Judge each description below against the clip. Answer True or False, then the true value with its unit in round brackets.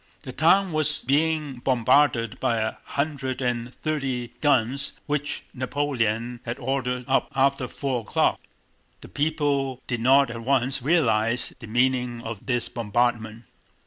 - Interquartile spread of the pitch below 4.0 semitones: True (3.0 semitones)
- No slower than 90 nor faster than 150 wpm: True (135 wpm)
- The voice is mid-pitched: False (130 Hz)